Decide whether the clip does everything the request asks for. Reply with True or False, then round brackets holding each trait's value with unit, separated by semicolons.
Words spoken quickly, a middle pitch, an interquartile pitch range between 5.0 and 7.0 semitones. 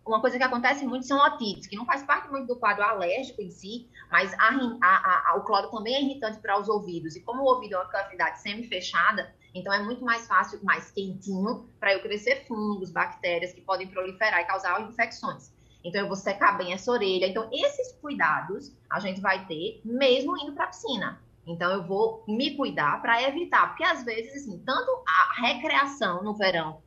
False (200 wpm; 215 Hz; 5.3 semitones)